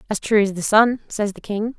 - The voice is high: Yes, high, 210 Hz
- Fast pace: Yes, fast, 270 wpm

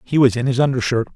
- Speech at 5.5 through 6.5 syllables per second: No, 7.0 syllables/s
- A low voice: Yes, low, 125 Hz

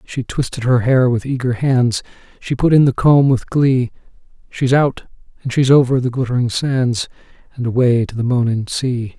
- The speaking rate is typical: Yes, average, 185 wpm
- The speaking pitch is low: Yes, low, 125 Hz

